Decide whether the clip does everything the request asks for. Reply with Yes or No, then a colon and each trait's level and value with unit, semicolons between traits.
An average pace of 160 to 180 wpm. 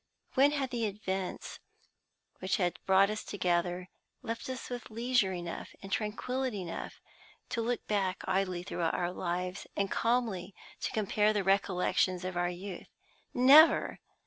No: average, 145 wpm